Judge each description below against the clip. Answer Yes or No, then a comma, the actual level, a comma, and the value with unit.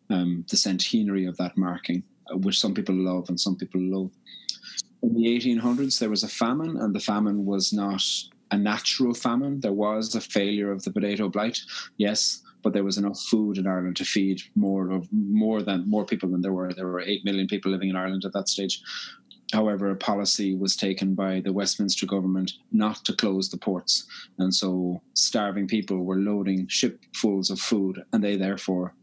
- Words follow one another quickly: No, average, 190 wpm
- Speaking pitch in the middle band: No, very low, 95 Hz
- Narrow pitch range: Yes, narrow, 1.8 semitones